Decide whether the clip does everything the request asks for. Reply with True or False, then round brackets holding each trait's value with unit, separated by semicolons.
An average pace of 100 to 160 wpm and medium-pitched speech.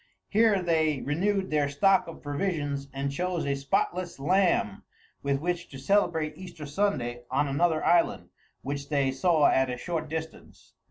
True (155 wpm; 155 Hz)